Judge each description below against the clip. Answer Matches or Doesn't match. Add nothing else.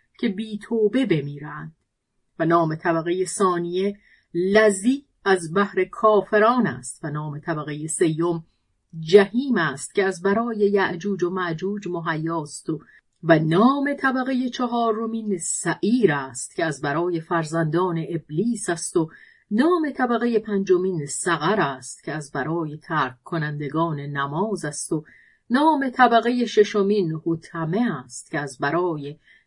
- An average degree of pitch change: Matches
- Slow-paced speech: Doesn't match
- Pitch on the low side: Doesn't match